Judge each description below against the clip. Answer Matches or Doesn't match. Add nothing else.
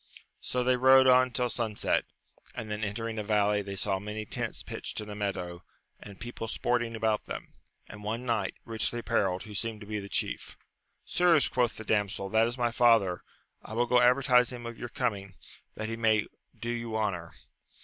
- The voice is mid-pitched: Doesn't match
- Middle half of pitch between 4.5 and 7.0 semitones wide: Doesn't match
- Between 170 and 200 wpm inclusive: Matches